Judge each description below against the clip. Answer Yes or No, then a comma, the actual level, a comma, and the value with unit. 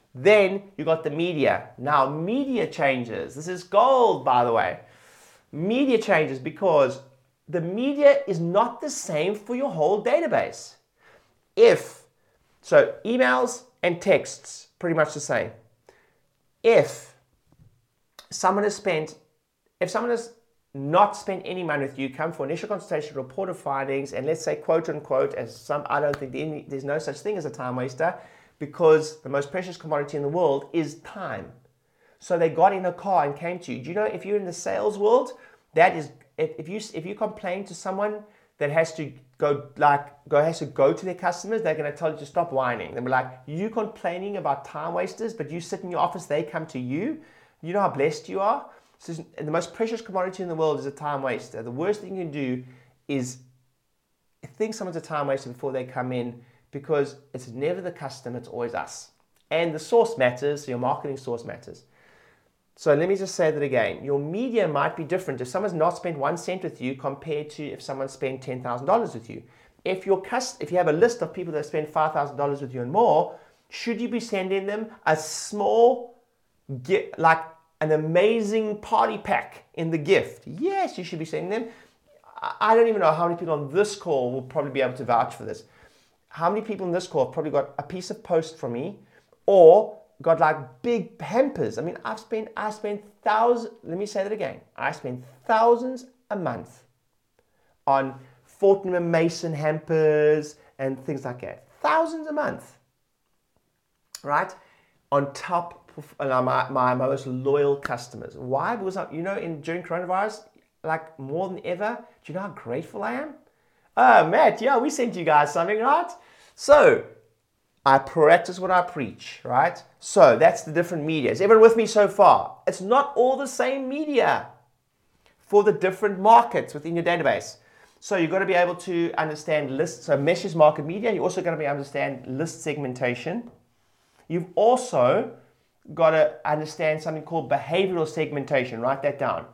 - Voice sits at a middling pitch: Yes, medium, 165 Hz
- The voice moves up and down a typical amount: No, wide, 6.4 semitones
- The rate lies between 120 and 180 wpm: No, average, 190 wpm